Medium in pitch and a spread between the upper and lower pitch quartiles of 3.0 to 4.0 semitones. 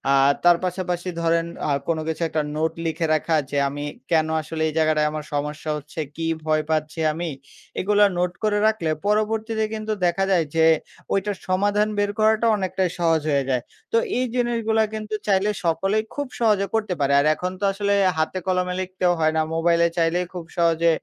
No: medium, 175 Hz; average, 4.4 semitones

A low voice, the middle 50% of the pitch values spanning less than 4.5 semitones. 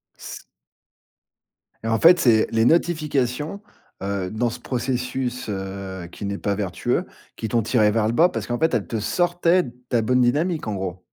No: low, 120 Hz; wide, 5.6 semitones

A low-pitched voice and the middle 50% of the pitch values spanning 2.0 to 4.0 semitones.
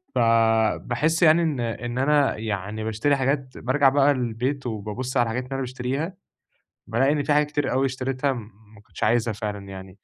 Yes: low, 125 Hz; average, 3.7 semitones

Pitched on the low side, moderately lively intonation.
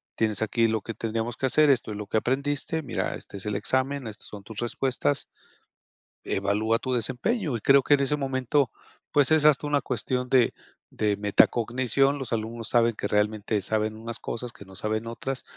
Yes: low, 115 Hz; average, 3.8 semitones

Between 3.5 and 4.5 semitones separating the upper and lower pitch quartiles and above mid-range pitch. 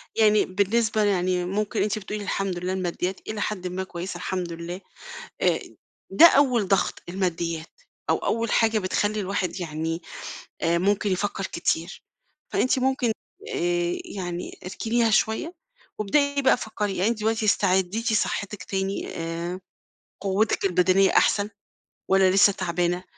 No: average, 3.1 semitones; high, 195 Hz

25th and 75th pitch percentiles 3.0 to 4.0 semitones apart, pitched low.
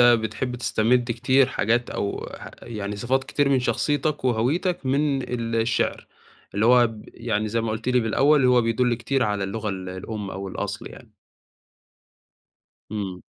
Yes: average, 3.4 semitones; low, 120 Hz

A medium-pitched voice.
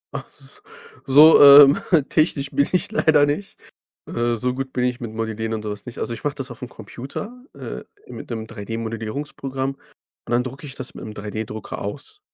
No: low, 125 Hz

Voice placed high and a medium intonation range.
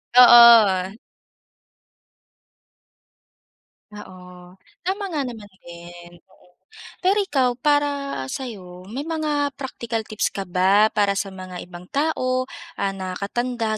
No: high, 215 Hz; wide, 5.9 semitones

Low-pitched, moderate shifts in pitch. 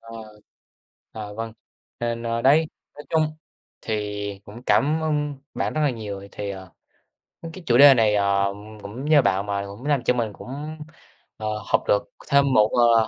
No: low, 115 Hz; wide, 5.7 semitones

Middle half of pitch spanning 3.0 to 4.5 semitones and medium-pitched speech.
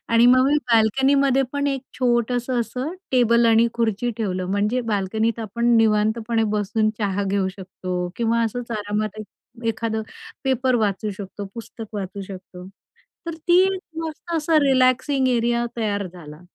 No: average, 3.5 semitones; high, 230 Hz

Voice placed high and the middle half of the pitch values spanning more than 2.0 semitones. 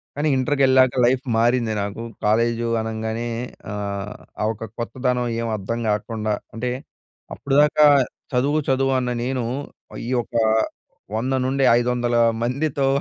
No: low, 120 Hz; average, 2.7 semitones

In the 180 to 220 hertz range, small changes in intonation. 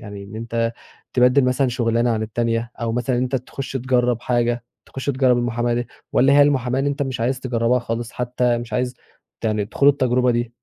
No: low, 120 Hz; narrow, 1.5 semitones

